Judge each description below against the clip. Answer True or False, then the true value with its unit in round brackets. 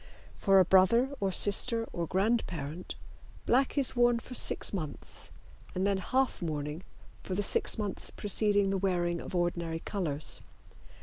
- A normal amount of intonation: True (4.4 semitones)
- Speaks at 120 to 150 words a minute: True (145 wpm)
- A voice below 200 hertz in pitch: True (190 Hz)